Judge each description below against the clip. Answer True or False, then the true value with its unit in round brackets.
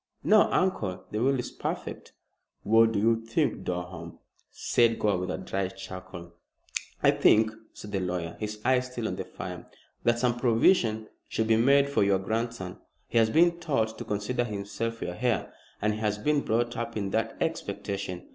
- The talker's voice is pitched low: True (110 Hz)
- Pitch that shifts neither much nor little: True (3.6 semitones)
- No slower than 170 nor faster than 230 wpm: True (175 wpm)